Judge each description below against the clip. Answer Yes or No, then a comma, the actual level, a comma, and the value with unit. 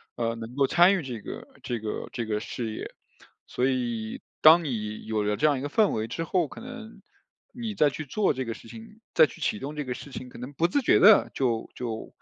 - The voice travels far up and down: Yes, wide, 7.1 semitones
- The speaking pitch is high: No, low, 130 Hz